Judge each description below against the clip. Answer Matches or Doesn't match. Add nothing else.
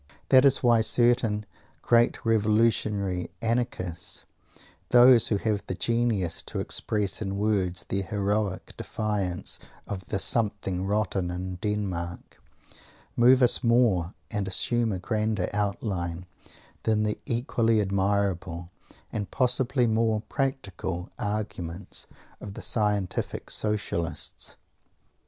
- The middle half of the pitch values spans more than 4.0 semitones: Doesn't match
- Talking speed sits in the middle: Doesn't match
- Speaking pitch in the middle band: Doesn't match